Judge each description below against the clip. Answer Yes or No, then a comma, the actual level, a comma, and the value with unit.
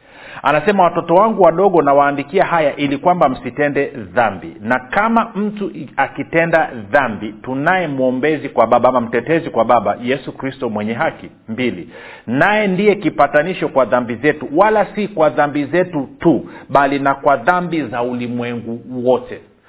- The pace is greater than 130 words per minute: Yes, fast, 140 wpm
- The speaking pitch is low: No, medium, 145 Hz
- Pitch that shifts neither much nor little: No, wide, 5.8 semitones